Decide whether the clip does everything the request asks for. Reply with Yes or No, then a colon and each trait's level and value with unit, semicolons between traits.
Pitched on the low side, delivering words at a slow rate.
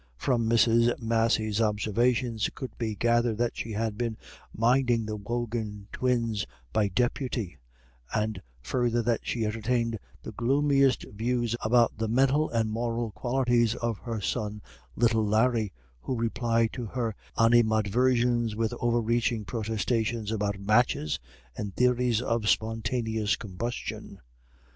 Yes: low, 115 Hz; slow, 130 wpm